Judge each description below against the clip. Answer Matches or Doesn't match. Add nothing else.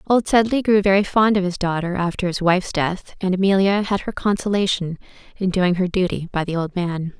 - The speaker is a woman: Matches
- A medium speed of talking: Doesn't match